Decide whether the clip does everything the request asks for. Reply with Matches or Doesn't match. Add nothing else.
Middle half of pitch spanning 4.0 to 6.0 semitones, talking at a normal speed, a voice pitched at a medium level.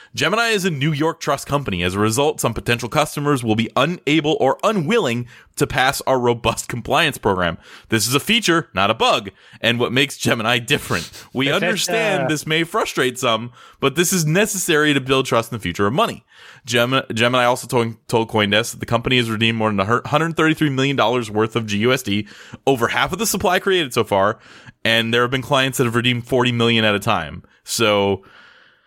Doesn't match